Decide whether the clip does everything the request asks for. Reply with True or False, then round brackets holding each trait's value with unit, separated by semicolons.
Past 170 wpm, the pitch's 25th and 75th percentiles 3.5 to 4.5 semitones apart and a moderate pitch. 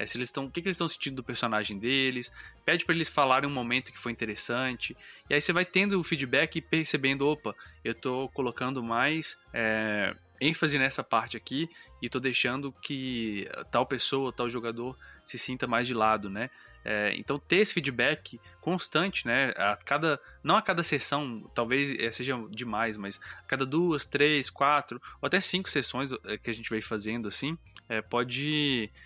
False (185 wpm; 4.1 semitones; 130 Hz)